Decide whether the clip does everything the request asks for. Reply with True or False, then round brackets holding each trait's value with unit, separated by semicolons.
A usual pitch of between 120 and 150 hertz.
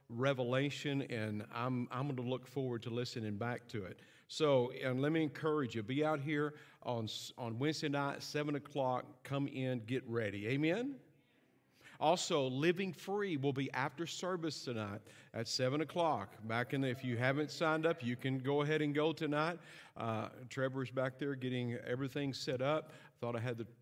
True (135 Hz)